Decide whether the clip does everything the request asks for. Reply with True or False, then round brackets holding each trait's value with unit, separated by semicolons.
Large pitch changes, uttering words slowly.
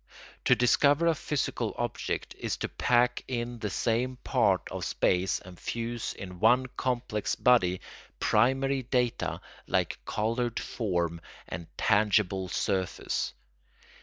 False (4.4 semitones; 120 wpm)